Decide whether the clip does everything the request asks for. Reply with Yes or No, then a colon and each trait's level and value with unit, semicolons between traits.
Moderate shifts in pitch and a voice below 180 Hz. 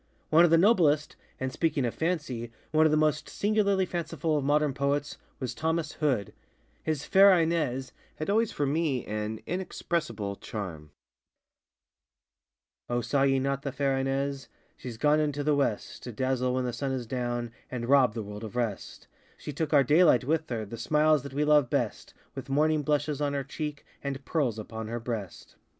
Yes: average, 4.2 semitones; medium, 140 Hz